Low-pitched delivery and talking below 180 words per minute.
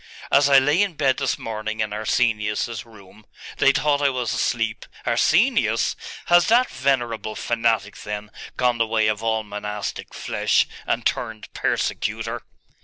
Yes: low, 115 Hz; average, 150 wpm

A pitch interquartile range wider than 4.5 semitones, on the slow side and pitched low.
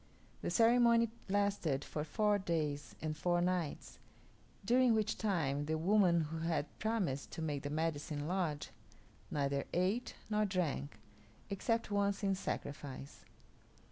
No: wide, 5.6 semitones; slow, 130 wpm; medium, 175 Hz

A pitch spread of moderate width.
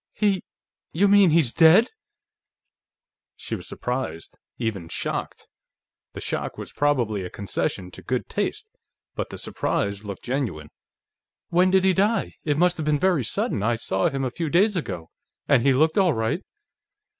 No: wide, 8.2 semitones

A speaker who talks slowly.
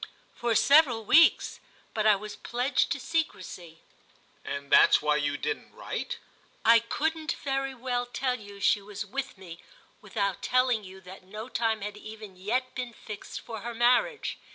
No: average, 160 wpm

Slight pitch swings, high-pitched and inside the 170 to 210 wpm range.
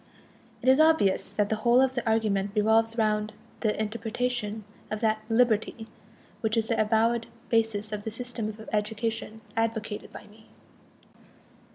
No: narrow, 1.4 semitones; high, 220 Hz; average, 150 wpm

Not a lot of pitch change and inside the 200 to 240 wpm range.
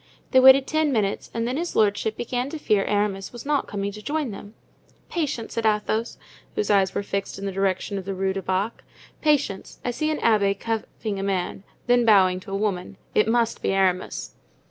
No: average, 3.7 semitones; fast, 205 wpm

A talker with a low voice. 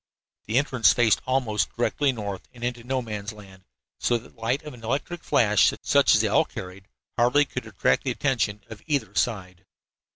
Yes: low, 115 Hz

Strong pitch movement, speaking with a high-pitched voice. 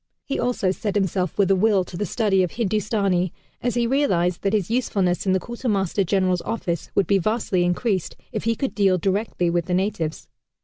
No: average, 3.2 semitones; high, 195 Hz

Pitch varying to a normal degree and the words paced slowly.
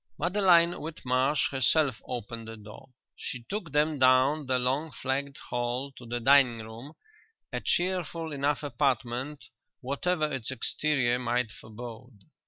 Yes: average, 3.7 semitones; slow, 130 wpm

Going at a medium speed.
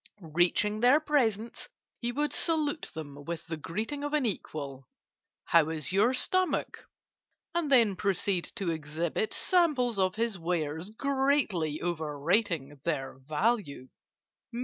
No: slow, 125 wpm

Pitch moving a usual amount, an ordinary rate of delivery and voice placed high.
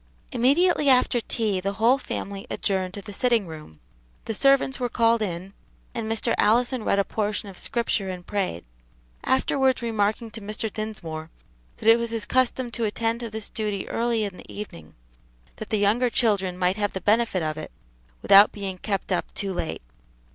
Yes: average, 3.3 semitones; average, 180 wpm; high, 215 Hz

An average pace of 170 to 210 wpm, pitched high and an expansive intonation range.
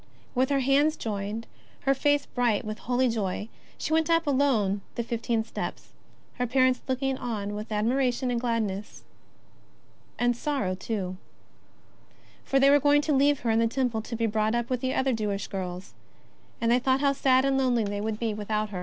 No: average, 190 wpm; high, 240 Hz; average, 3.9 semitones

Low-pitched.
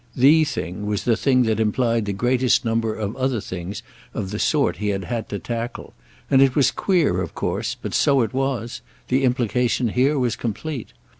Yes: low, 120 Hz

